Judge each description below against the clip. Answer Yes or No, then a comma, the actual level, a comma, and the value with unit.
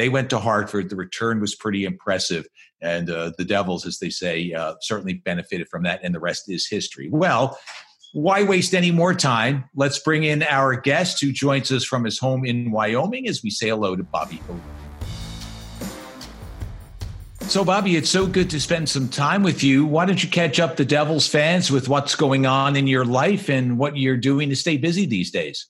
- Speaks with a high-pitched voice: No, low, 135 Hz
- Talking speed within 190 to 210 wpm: Yes, average, 200 wpm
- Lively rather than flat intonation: Yes, wide, 7.0 semitones